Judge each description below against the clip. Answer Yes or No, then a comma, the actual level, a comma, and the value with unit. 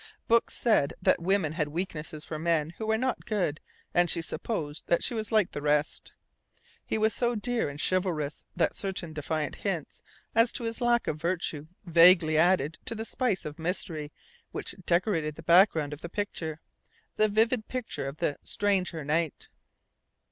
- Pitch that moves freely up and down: Yes, wide, 5.7 semitones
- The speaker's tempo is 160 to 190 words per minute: Yes, average, 175 wpm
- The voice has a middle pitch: Yes, medium, 170 Hz